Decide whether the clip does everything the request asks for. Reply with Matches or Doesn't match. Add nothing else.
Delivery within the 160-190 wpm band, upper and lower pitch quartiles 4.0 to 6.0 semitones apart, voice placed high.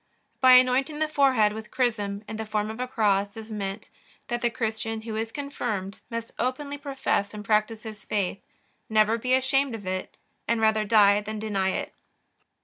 Doesn't match